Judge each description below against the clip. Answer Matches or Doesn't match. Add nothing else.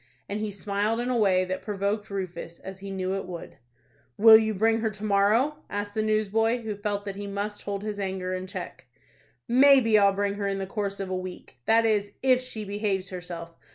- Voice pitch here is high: Matches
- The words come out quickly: Matches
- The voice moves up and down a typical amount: Doesn't match